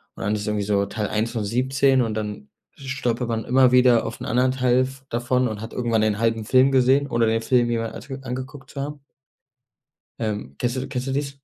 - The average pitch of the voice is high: No, low, 120 Hz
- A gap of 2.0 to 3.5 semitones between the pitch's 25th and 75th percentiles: Yes, average, 2.9 semitones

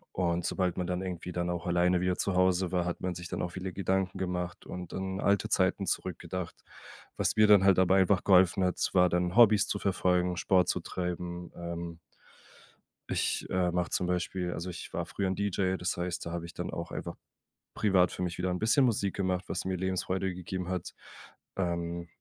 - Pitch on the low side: Yes, very low, 90 Hz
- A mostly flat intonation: Yes, narrow, 1.3 semitones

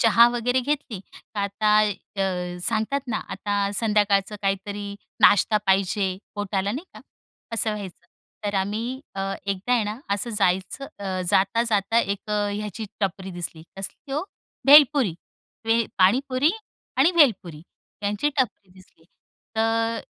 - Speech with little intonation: No, average, 3.2 semitones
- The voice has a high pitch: Yes, high, 205 Hz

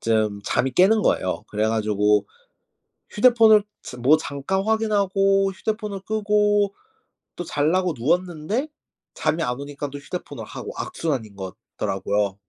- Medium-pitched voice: Yes, medium, 165 Hz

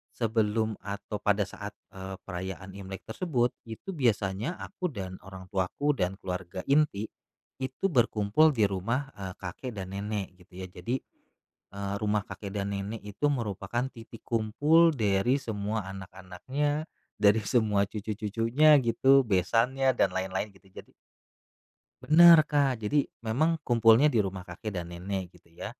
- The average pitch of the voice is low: Yes, low, 105 Hz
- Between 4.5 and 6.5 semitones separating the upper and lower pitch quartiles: Yes, average, 4.8 semitones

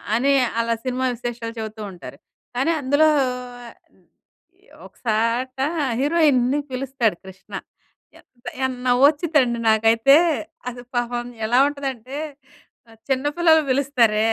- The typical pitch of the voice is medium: No, very high, 250 Hz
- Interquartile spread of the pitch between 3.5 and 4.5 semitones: No, average, 3.0 semitones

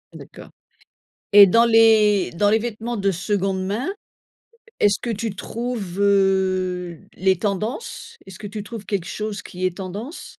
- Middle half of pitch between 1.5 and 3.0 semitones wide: Yes, average, 2.7 semitones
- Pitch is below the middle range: No, high, 200 Hz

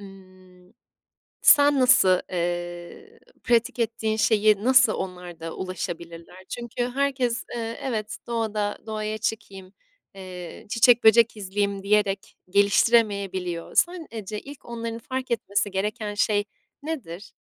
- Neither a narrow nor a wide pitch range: Yes, average, 3.9 semitones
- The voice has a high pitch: Yes, high, 210 Hz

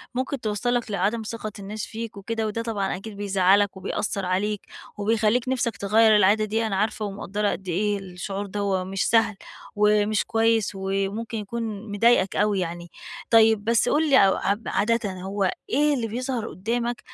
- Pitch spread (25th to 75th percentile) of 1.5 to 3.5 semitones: Yes, narrow, 2.5 semitones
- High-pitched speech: Yes, high, 210 Hz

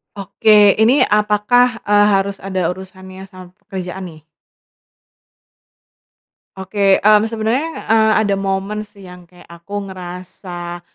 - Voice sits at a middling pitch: No, high, 195 Hz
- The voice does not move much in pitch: Yes, narrow, 2.3 semitones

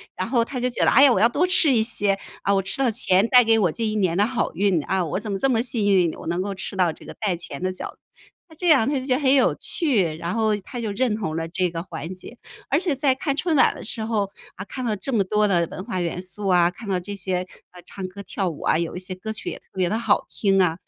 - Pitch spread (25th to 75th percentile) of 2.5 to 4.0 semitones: No, average, 4.7 semitones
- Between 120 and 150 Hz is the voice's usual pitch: No, high, 205 Hz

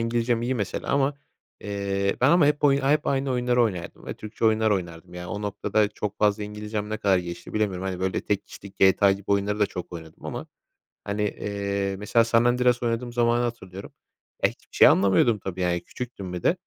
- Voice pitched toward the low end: Yes, low, 105 Hz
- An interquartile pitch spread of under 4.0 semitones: Yes, average, 3.5 semitones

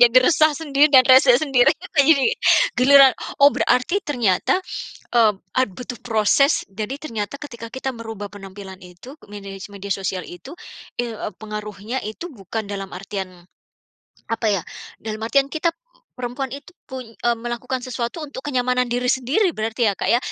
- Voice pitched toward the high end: Yes, high, 245 Hz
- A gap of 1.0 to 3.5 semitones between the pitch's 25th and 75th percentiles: No, average, 4.4 semitones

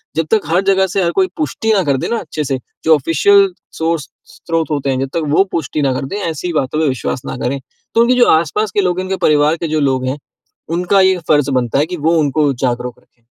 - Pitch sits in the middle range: Yes, medium, 160 Hz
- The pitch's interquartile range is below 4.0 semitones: No, average, 5.1 semitones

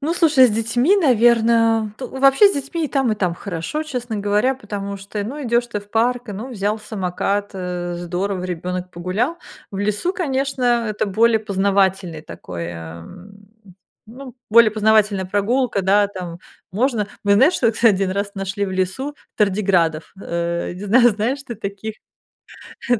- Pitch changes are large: No, average, 4.1 semitones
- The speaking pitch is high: Yes, high, 210 Hz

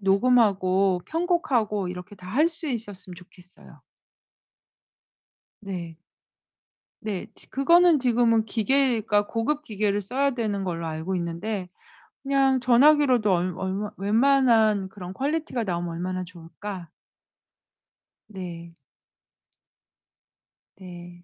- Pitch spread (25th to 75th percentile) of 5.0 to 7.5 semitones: Yes, wide, 5.4 semitones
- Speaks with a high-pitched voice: Yes, high, 205 Hz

